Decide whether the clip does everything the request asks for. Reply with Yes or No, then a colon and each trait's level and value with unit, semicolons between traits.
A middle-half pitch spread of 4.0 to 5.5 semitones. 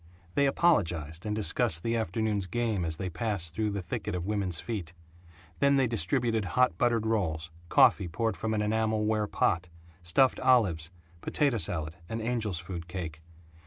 Yes: average, 4.7 semitones